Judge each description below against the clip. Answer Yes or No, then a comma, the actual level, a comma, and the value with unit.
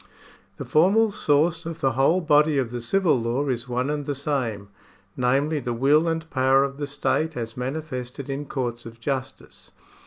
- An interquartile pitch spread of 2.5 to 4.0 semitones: Yes, average, 3.5 semitones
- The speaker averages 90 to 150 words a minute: No, average, 180 wpm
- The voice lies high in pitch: No, medium, 140 Hz